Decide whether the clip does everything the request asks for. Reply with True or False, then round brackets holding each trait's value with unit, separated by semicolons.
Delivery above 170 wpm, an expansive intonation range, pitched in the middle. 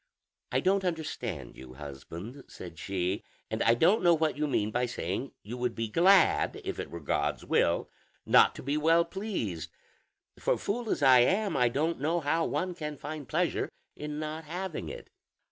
True (180 wpm; 7.0 semitones; 150 Hz)